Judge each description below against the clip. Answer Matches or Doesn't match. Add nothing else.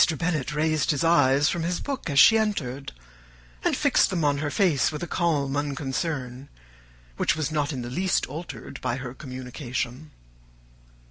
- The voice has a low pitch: Doesn't match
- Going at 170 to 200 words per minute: Doesn't match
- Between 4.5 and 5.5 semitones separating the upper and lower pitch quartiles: Doesn't match